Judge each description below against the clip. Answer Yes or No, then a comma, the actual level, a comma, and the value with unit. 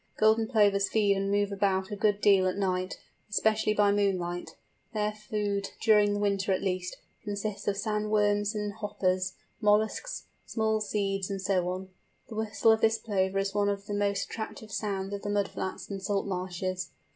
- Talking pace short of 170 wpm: No, average, 180 wpm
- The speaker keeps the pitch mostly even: Yes, narrow, 1.5 semitones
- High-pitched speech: Yes, high, 205 Hz